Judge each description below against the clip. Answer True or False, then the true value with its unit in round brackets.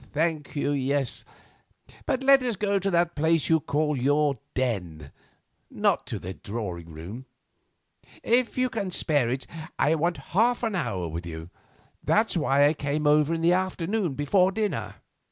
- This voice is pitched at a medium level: True (150 Hz)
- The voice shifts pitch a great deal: True (6.5 semitones)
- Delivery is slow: False (160 wpm)